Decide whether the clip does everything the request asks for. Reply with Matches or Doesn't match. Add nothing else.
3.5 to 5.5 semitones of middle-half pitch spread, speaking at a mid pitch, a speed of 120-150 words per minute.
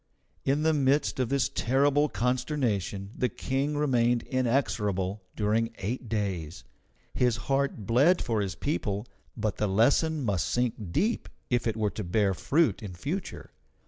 Doesn't match